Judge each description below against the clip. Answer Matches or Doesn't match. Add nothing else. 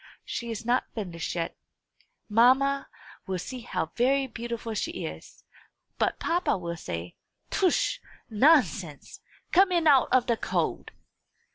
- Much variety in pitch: Matches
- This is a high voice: Matches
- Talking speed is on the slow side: Matches